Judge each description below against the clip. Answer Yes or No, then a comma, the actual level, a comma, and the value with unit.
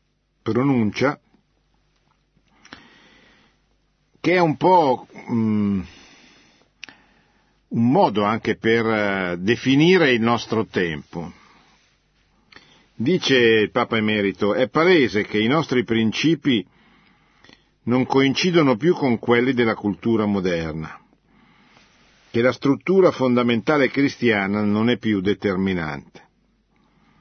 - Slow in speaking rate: Yes, slow, 90 wpm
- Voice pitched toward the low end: Yes, low, 115 Hz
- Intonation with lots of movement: No, average, 4.2 semitones